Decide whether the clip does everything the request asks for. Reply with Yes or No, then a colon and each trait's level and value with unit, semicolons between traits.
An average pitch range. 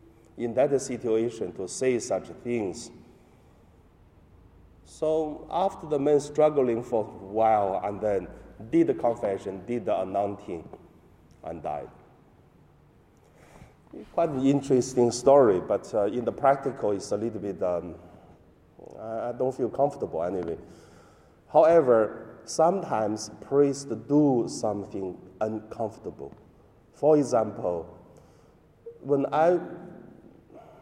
No: wide, 5.8 semitones